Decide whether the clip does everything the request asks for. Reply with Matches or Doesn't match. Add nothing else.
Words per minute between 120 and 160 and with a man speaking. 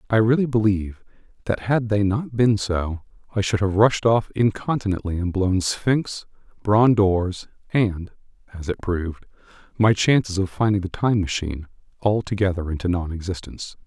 Matches